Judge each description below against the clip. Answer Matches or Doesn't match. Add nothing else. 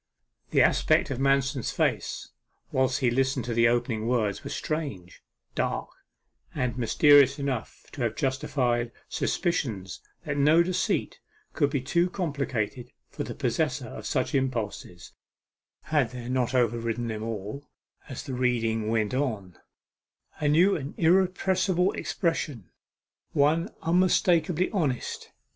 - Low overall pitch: Matches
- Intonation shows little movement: Doesn't match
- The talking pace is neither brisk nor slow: Doesn't match